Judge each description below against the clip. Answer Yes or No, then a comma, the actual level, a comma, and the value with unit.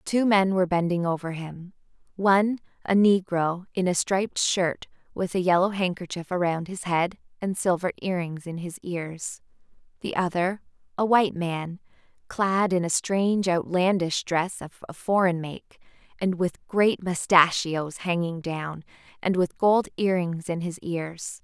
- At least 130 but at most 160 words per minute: Yes, average, 150 wpm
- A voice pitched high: No, medium, 180 Hz